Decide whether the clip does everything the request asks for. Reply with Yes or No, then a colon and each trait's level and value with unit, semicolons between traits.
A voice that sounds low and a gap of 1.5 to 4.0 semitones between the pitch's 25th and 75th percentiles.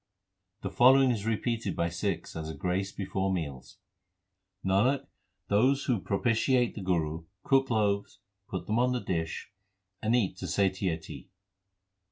No: low, 100 Hz; average, 4.7 semitones